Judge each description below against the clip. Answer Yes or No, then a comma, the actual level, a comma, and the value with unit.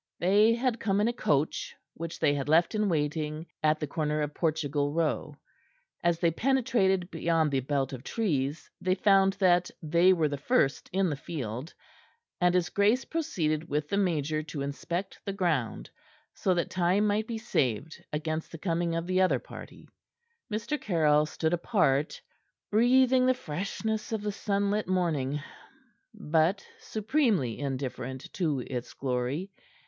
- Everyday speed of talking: Yes, average, 155 wpm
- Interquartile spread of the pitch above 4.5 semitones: Yes, average, 5.2 semitones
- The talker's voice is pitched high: No, medium, 170 Hz